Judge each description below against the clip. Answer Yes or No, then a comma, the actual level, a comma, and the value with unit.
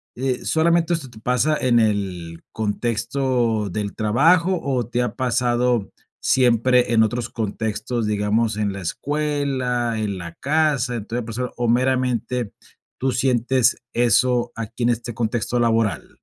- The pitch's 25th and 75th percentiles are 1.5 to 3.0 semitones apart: Yes, narrow, 2.6 semitones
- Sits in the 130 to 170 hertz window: No, low, 120 Hz